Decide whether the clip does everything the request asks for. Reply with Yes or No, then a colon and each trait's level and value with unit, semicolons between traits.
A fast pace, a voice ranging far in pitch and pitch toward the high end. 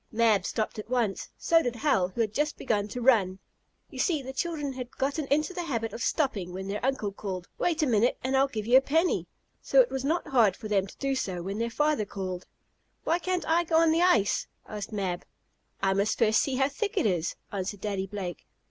Yes: fast, 230 wpm; wide, 6.3 semitones; high, 235 Hz